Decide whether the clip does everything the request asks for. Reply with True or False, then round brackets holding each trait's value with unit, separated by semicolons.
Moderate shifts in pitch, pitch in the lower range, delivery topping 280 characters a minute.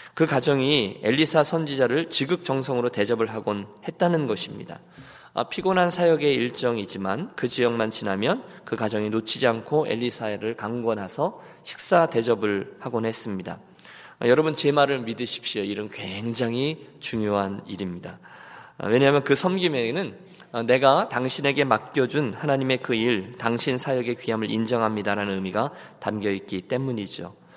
True (4.8 semitones; 120 Hz; 320 characters per minute)